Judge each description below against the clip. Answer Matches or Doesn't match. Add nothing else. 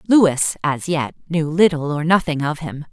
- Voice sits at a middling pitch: Matches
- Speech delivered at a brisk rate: Doesn't match